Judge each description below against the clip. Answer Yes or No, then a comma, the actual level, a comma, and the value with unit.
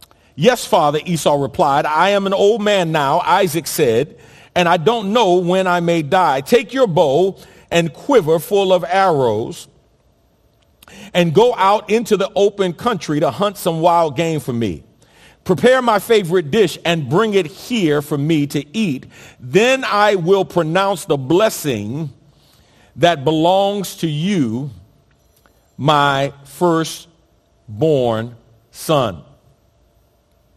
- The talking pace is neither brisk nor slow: No, slow, 130 wpm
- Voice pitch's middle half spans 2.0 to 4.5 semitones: No, average, 5.2 semitones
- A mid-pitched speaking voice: Yes, medium, 170 Hz